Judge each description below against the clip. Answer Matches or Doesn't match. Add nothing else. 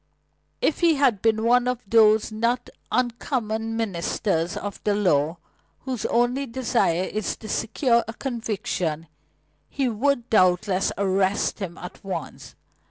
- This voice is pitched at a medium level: Doesn't match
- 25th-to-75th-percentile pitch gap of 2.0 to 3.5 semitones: Doesn't match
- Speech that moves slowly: Matches